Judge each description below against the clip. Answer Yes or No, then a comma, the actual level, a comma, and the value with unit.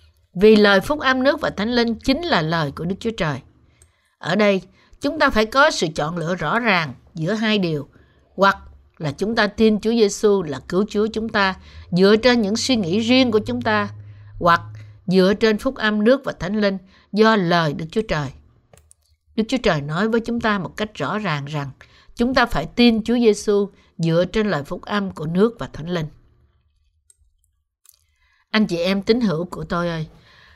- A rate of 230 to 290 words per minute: No, average, 195 wpm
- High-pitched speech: Yes, high, 195 Hz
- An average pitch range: No, wide, 7.1 semitones